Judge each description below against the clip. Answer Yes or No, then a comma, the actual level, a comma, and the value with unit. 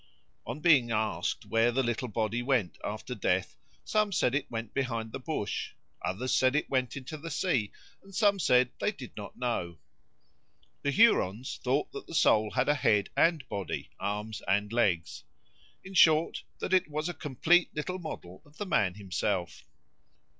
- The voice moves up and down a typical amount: No, wide, 6.2 semitones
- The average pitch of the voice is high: No, low, 125 Hz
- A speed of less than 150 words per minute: No, average, 170 wpm